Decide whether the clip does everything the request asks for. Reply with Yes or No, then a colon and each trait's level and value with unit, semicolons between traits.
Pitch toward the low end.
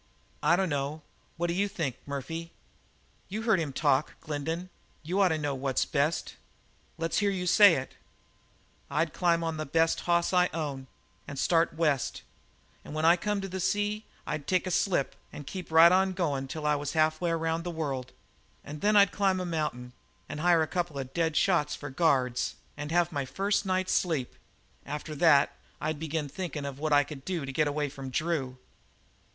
No: medium, 160 Hz